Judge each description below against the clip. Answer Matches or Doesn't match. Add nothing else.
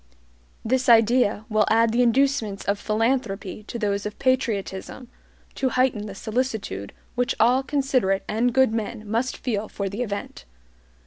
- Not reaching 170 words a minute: Matches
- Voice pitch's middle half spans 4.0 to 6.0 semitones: Doesn't match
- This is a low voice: Doesn't match